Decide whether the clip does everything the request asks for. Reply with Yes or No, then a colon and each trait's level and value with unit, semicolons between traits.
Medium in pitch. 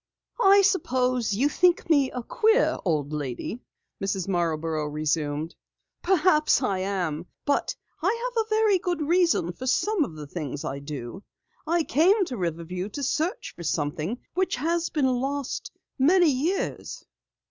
No: very high, 255 Hz